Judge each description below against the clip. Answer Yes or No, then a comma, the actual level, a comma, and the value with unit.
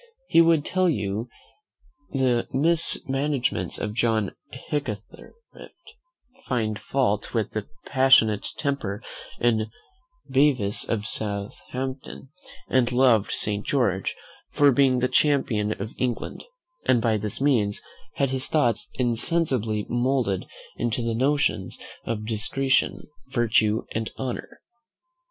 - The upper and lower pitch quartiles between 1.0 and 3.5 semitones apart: No, average, 4.0 semitones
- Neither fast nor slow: No, slow, 110 wpm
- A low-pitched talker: Yes, low, 120 Hz